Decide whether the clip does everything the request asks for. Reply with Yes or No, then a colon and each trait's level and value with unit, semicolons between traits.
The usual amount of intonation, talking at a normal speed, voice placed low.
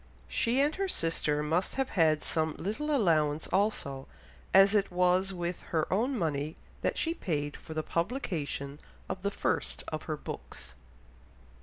No: average, 5.0 semitones; average, 155 wpm; medium, 175 Hz